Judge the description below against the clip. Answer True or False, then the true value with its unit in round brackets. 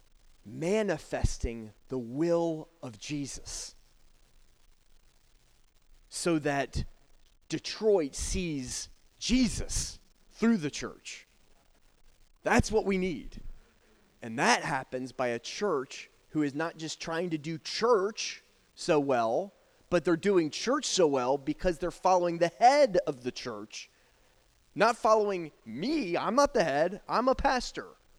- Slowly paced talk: True (120 wpm)